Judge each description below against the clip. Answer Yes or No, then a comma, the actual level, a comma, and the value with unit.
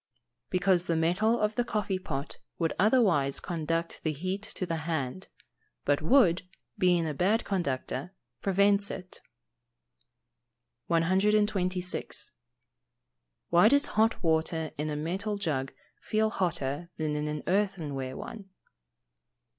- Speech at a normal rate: No, slow, 125 wpm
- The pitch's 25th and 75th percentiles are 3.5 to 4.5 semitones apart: Yes, average, 4.1 semitones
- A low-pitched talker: No, medium, 180 Hz